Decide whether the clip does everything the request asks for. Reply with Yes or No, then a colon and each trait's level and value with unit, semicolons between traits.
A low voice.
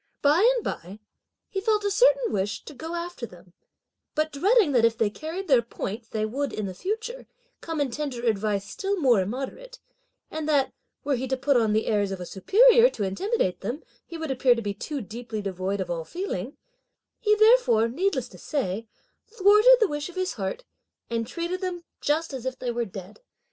No: very high, 275 Hz